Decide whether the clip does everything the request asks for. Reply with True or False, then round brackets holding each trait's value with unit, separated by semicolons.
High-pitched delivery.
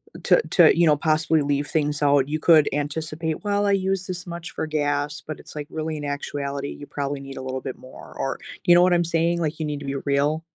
False (150 Hz)